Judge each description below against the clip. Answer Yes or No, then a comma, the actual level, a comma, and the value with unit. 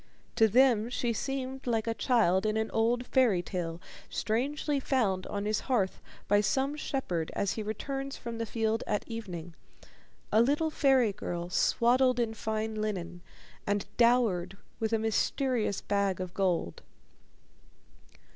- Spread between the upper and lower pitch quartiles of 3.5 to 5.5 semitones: Yes, average, 3.8 semitones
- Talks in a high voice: Yes, high, 220 Hz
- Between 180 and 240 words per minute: No, average, 145 wpm